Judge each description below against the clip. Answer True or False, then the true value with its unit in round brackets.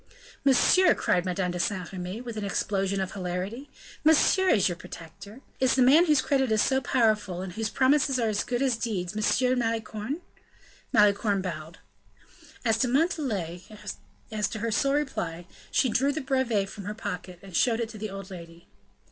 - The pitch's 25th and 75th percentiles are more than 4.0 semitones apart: True (5.5 semitones)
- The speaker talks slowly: False (175 wpm)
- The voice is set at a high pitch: True (215 Hz)